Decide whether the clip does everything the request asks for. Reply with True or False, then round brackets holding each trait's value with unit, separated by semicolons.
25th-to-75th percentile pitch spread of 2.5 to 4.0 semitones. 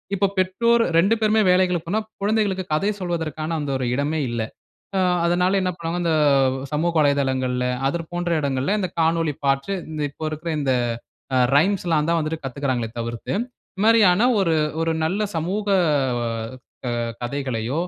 False (4.8 semitones)